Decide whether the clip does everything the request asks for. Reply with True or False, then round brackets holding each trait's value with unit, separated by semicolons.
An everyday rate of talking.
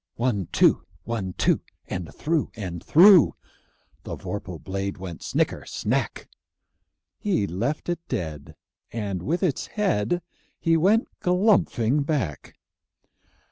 False (115 wpm)